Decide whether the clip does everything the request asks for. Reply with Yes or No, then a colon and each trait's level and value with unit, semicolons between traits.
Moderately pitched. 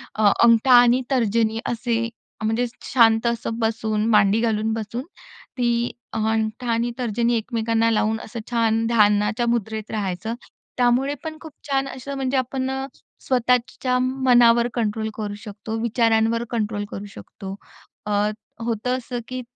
No: high, 230 Hz